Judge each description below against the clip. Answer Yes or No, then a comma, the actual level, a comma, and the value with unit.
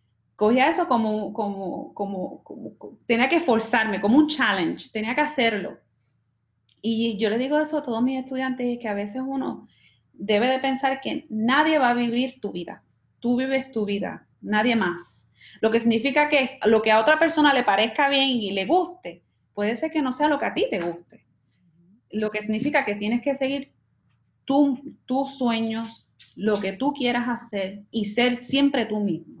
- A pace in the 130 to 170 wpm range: No, fast, 190 wpm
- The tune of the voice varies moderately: Yes, average, 4.5 semitones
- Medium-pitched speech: No, high, 235 Hz